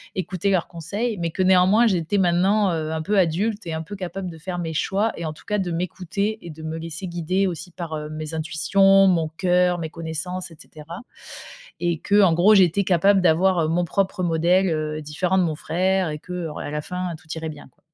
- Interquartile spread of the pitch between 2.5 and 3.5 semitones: Yes, average, 2.9 semitones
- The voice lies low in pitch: No, medium, 175 Hz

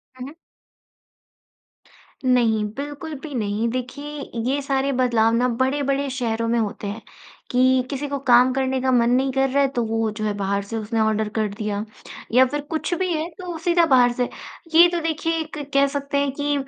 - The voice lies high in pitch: Yes, very high, 260 Hz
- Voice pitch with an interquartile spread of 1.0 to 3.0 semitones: No, average, 3.8 semitones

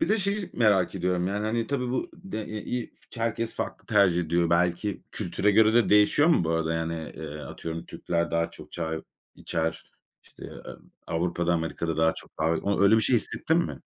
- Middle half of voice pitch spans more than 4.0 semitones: Yes, average, 5.2 semitones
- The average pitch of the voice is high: No, very low, 90 Hz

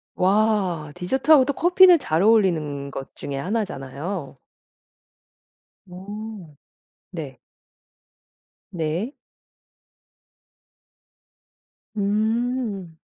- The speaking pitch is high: Yes, high, 195 Hz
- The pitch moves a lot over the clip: Yes, wide, 6.1 semitones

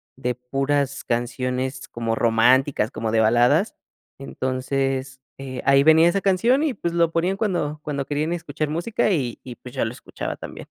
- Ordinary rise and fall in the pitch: Yes, average, 4.7 semitones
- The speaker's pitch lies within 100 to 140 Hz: Yes, low, 135 Hz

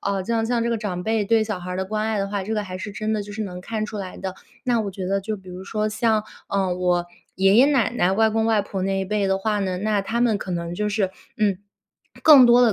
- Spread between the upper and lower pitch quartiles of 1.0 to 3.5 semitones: Yes, narrow, 2.6 semitones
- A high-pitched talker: Yes, high, 205 Hz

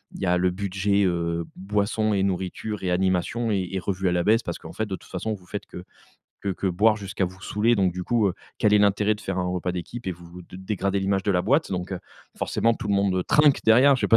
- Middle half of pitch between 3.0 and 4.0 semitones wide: No, narrow, 2.6 semitones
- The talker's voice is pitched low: Yes, very low, 95 Hz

